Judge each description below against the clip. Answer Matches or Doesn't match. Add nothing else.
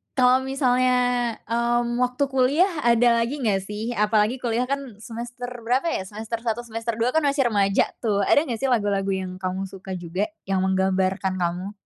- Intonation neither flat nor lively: Matches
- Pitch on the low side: Doesn't match